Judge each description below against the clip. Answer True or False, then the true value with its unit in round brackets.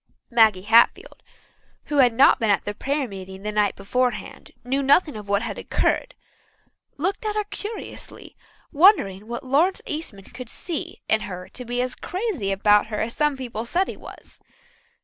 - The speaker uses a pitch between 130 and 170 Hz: False (245 Hz)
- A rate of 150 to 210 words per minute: True (170 wpm)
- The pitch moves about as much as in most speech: False (6.3 semitones)